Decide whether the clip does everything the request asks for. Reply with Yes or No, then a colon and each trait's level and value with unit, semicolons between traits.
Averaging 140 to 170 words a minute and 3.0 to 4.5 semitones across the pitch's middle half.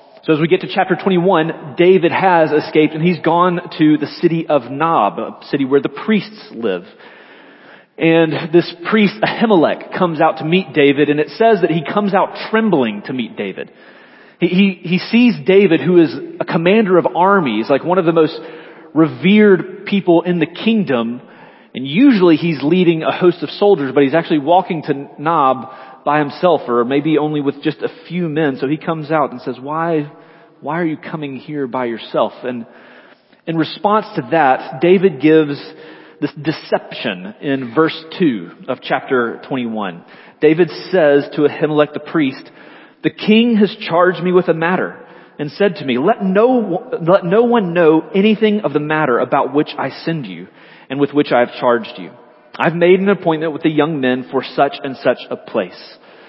No: average, 185 wpm; average, 3.9 semitones